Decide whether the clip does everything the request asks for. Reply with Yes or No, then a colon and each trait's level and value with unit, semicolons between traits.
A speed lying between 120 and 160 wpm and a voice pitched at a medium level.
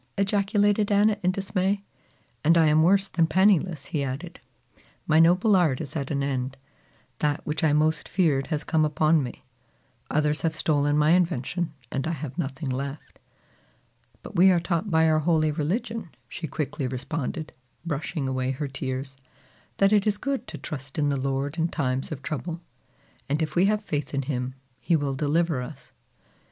No: average, 175 wpm; medium, 155 Hz